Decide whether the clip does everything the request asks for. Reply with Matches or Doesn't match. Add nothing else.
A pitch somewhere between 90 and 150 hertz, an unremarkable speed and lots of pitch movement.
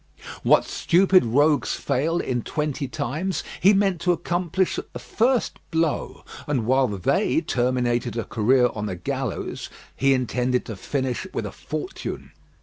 Matches